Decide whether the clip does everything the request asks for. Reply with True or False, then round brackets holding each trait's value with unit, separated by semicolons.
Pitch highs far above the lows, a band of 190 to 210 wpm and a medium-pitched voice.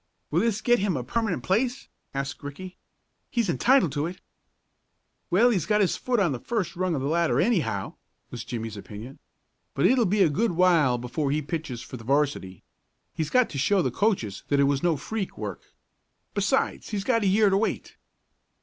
True (7.3 semitones; 195 wpm; 170 Hz)